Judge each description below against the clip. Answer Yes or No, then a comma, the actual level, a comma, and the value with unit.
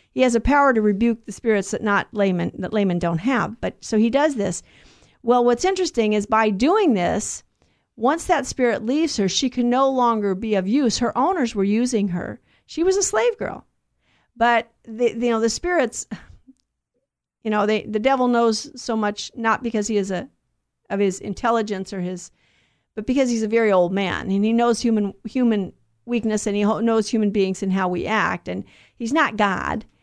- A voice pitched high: Yes, high, 225 Hz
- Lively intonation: No, average, 3.3 semitones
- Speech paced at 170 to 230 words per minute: Yes, average, 200 wpm